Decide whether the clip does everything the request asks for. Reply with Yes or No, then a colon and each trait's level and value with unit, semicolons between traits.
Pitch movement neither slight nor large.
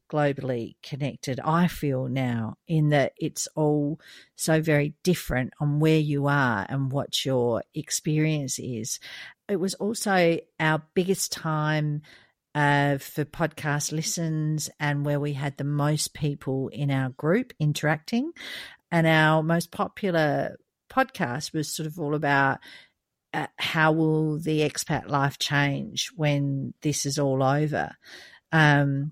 No: narrow, 2.0 semitones